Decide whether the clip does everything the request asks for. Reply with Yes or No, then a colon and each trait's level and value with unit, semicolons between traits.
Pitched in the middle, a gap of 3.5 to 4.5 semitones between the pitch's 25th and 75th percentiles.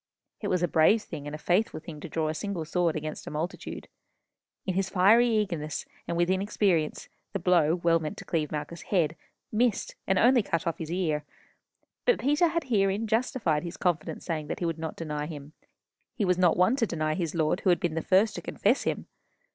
Yes: medium, 175 Hz; average, 4.1 semitones